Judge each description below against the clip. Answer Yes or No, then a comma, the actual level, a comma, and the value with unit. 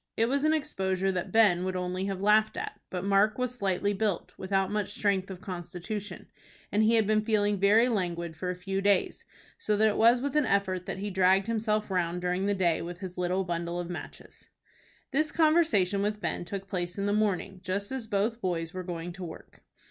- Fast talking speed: Yes, fast, 210 wpm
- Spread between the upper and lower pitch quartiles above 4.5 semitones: No, average, 2.9 semitones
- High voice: Yes, high, 195 Hz